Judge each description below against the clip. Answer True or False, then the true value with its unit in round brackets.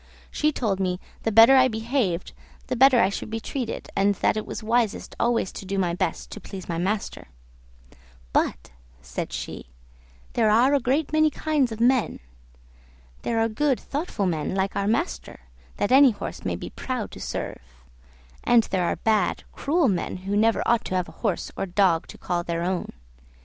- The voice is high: True (215 Hz)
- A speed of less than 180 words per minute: False (185 wpm)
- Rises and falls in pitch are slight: False (4.9 semitones)